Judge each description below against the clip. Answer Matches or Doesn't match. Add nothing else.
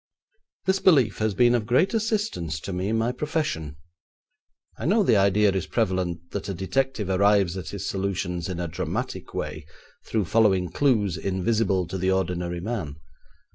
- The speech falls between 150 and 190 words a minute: Matches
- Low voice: Matches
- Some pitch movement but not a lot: Matches